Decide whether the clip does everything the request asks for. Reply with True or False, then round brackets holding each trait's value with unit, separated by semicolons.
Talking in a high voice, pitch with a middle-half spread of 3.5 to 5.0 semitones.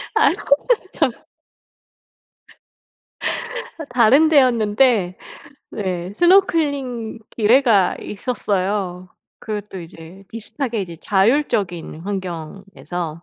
False (210 Hz; 5.4 semitones)